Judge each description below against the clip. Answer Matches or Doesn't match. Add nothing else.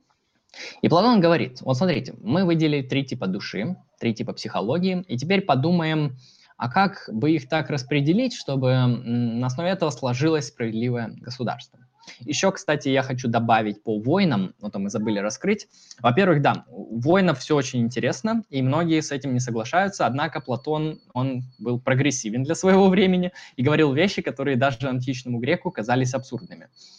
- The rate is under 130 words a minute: Doesn't match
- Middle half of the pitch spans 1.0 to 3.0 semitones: Doesn't match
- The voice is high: Doesn't match